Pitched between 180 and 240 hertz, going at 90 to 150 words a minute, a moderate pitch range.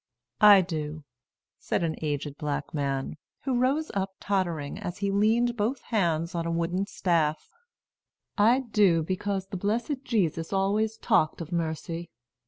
Yes: medium, 185 Hz; average, 145 wpm; average, 4.8 semitones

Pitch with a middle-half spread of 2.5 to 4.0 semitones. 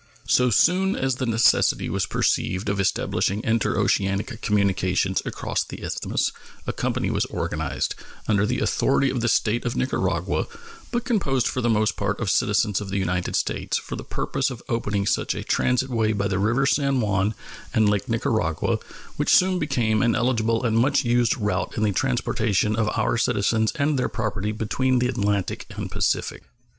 Yes: average, 3.5 semitones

